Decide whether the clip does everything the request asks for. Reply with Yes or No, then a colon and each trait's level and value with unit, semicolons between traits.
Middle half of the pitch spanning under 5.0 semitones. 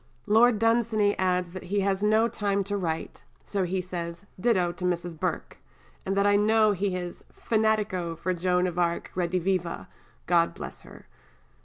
Yes: average, 2.8 semitones